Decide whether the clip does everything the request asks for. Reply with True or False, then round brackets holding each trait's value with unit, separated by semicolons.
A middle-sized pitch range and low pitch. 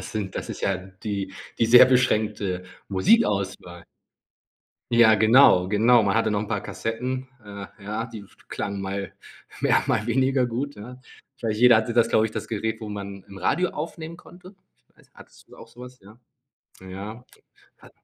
True (3.7 semitones; 110 Hz)